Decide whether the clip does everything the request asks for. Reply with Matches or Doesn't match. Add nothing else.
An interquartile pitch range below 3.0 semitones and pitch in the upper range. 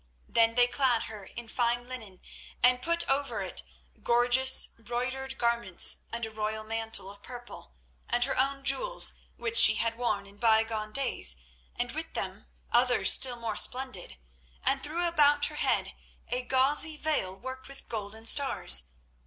Doesn't match